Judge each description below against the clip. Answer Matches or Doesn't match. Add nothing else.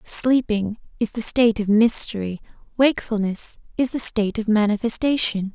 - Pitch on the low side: Doesn't match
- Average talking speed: Doesn't match